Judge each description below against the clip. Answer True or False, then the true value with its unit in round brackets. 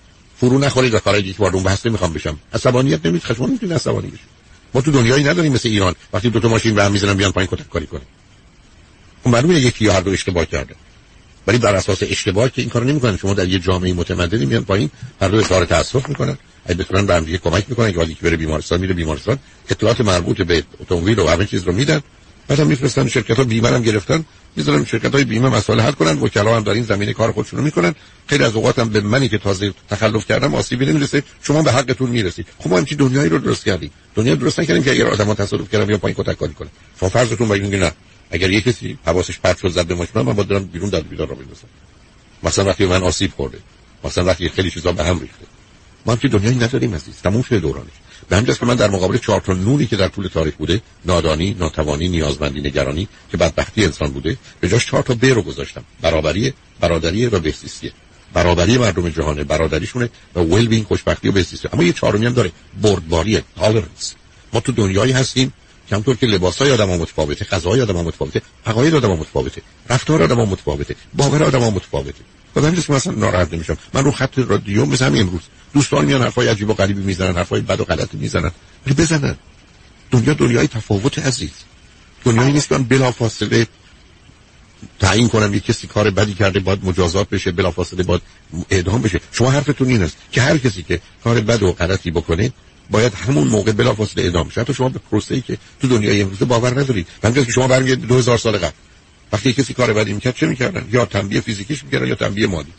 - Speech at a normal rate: False (210 wpm)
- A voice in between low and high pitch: False (105 Hz)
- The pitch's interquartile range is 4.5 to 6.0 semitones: True (5.2 semitones)